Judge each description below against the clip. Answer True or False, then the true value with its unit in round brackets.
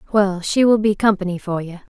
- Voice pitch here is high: True (195 Hz)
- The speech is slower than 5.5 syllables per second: False (5.7 syllables/s)